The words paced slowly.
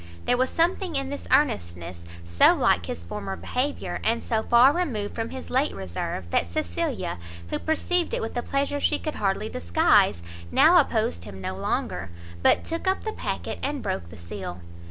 No: average, 180 wpm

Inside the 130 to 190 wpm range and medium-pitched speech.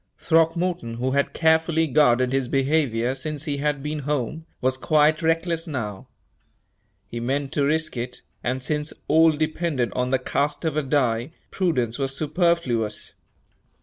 Yes: average, 150 wpm; medium, 145 Hz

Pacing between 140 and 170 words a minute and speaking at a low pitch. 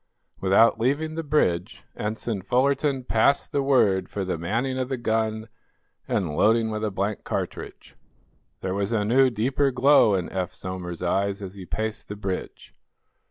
Yes: average, 160 wpm; low, 110 Hz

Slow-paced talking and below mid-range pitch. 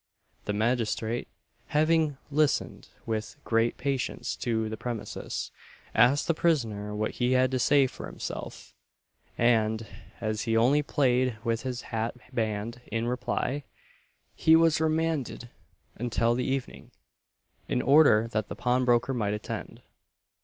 Yes: slow, 130 wpm; low, 120 Hz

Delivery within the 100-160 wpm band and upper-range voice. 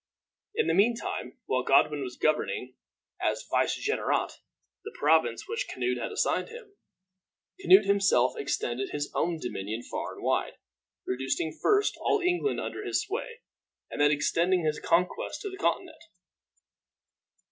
No: average, 140 wpm; medium, 180 Hz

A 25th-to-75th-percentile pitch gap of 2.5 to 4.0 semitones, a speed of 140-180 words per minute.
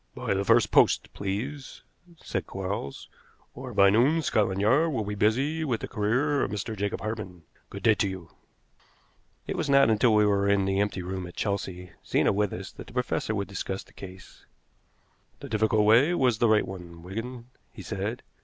No: average, 3.6 semitones; average, 190 wpm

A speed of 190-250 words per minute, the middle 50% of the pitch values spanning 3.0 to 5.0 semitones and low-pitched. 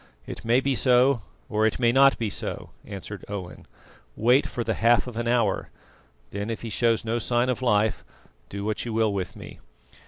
No: average, 195 wpm; narrow, 2.5 semitones; low, 115 Hz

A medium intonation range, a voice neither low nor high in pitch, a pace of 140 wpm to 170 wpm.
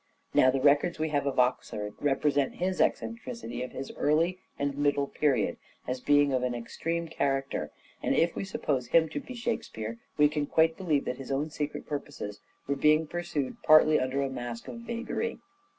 No: average, 3.6 semitones; medium, 145 Hz; average, 180 wpm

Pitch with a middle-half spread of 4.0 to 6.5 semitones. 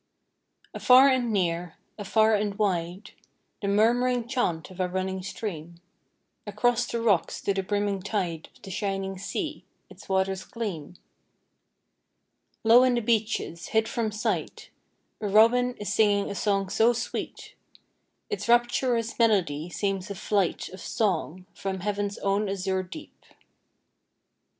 No: average, 3.2 semitones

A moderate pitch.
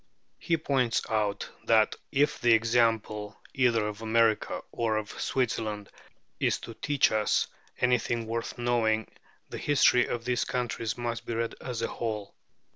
No: low, 115 Hz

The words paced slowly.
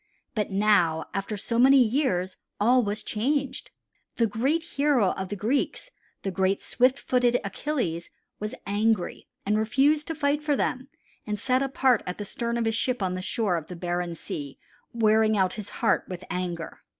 No: average, 175 wpm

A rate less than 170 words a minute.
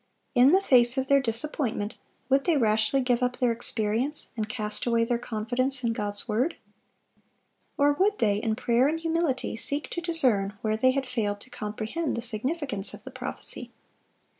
No: average, 175 wpm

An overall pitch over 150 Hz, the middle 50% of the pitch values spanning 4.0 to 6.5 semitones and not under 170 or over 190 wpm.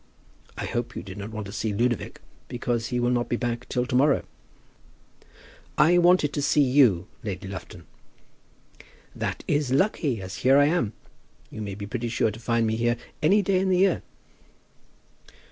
No: low, 120 Hz; average, 4.8 semitones; average, 180 wpm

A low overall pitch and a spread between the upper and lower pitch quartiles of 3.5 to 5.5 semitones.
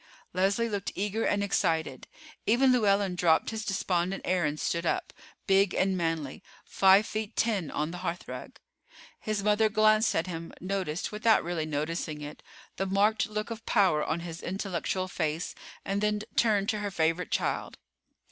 No: high, 195 Hz; average, 3.9 semitones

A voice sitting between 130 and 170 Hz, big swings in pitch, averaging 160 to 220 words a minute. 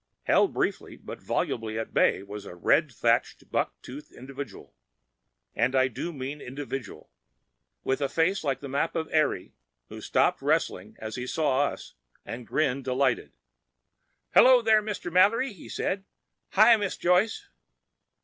No: medium, 140 Hz; wide, 6.0 semitones; average, 140 wpm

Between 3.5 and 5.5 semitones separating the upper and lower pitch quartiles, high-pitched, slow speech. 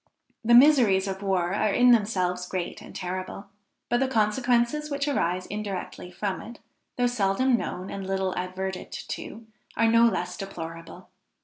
No: average, 4.3 semitones; high, 200 Hz; average, 150 wpm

